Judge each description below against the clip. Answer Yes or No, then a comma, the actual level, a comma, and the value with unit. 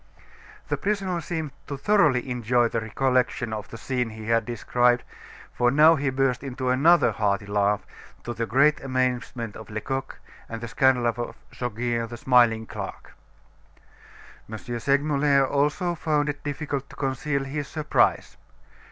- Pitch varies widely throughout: No, average, 3.5 semitones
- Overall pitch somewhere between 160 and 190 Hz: No, low, 130 Hz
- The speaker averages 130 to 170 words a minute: Yes, average, 150 wpm